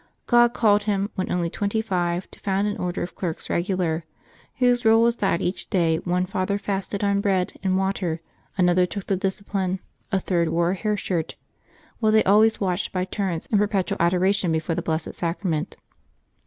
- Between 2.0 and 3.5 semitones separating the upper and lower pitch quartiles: Yes, narrow, 2.6 semitones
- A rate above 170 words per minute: Yes, average, 180 wpm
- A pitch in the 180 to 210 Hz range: Yes, high, 190 Hz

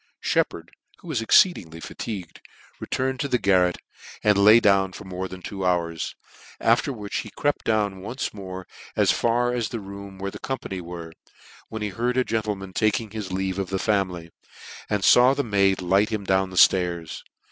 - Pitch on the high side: No, low, 100 Hz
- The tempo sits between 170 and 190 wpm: Yes, average, 180 wpm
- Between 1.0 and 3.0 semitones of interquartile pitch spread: No, average, 3.4 semitones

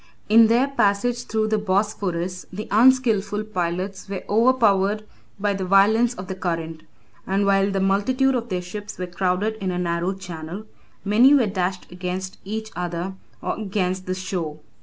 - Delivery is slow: No, average, 160 wpm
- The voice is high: Yes, high, 195 Hz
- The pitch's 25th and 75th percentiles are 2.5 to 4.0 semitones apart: Yes, average, 2.9 semitones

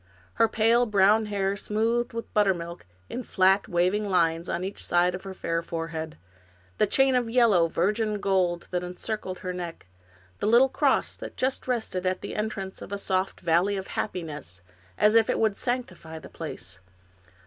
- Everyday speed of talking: Yes, average, 170 wpm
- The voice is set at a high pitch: Yes, high, 195 Hz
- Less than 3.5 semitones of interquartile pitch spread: No, average, 3.9 semitones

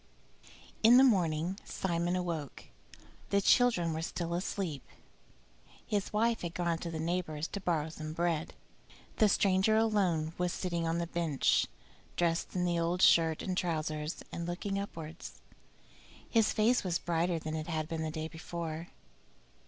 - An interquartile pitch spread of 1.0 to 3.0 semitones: Yes, narrow, 2.6 semitones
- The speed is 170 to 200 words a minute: No, average, 155 wpm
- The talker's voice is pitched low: No, medium, 170 Hz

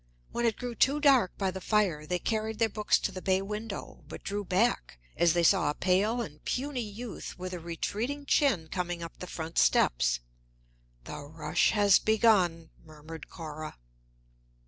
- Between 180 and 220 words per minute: No, average, 170 wpm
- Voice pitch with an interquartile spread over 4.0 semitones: Yes, average, 5.1 semitones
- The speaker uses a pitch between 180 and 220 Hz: Yes, high, 190 Hz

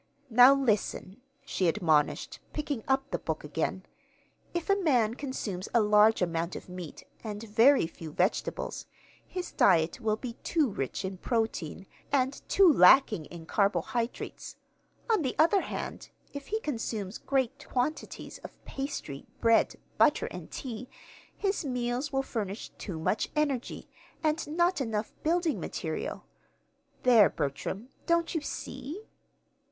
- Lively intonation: Yes, wide, 6.3 semitones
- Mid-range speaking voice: No, high, 240 Hz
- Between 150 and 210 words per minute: No, slow, 135 wpm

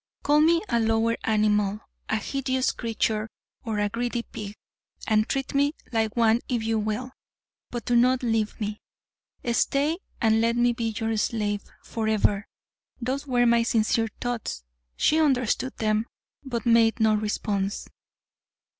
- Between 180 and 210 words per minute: No, average, 145 wpm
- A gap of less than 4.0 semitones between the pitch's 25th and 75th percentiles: Yes, narrow, 2.4 semitones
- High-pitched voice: Yes, high, 230 Hz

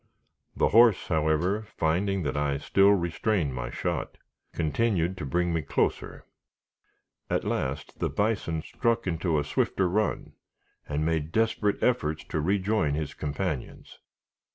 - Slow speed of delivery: Yes, slow, 130 wpm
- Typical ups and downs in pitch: Yes, average, 5.0 semitones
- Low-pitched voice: Yes, very low, 85 Hz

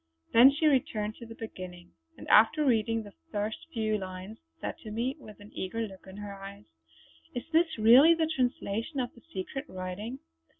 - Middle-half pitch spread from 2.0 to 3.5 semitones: No, average, 4.5 semitones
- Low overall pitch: No, high, 225 Hz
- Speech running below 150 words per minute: No, average, 180 wpm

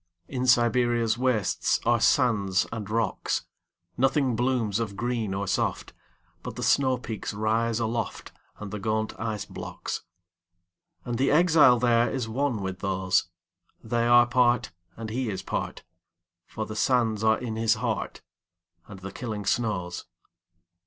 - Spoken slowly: Yes, slow, 115 wpm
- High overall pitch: No, low, 110 Hz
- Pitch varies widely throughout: No, average, 3.8 semitones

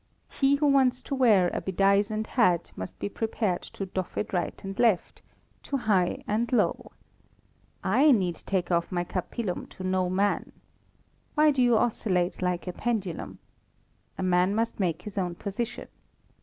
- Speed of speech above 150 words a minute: Yes, average, 160 wpm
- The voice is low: No, high, 195 Hz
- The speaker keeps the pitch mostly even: No, average, 4.5 semitones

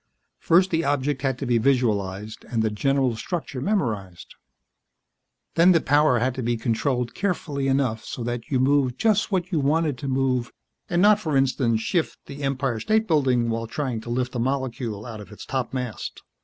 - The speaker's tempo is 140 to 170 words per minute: No, average, 185 wpm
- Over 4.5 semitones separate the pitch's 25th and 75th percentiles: No, average, 3.8 semitones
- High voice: No, low, 130 Hz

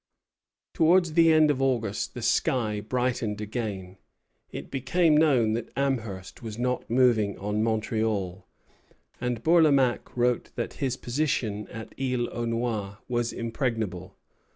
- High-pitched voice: No, low, 120 Hz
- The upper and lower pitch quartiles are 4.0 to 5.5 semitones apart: No, average, 3.5 semitones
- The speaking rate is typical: No, slow, 130 wpm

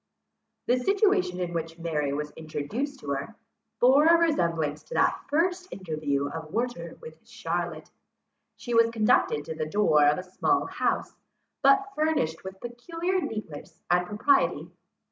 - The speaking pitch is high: Yes, high, 210 Hz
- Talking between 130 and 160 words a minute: Yes, average, 145 wpm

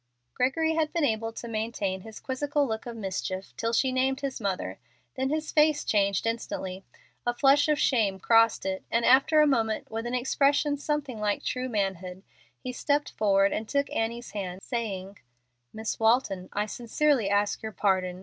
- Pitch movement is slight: No, average, 5.2 semitones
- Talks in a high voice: Yes, high, 230 Hz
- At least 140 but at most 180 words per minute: Yes, average, 175 wpm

